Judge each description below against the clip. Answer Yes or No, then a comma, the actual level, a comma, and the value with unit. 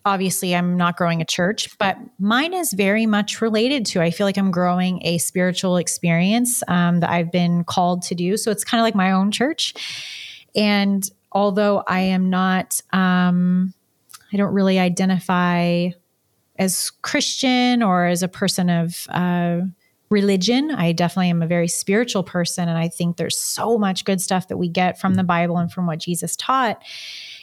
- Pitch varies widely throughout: No, narrow, 2.6 semitones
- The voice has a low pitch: No, medium, 185 Hz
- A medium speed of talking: Yes, average, 175 wpm